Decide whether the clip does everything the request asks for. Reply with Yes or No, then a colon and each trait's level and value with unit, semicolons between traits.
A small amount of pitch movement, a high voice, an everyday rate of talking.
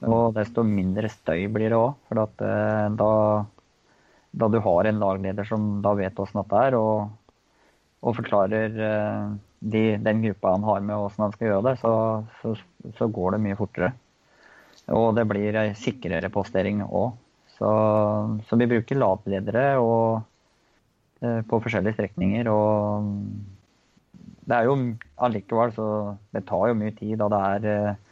No: narrow, 1.5 semitones; low, 105 Hz; average, 145 wpm